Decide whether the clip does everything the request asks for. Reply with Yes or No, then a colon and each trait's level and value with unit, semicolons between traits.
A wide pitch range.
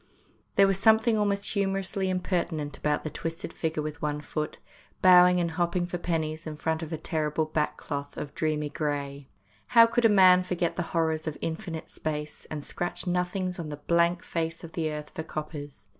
No: average, 3.0 semitones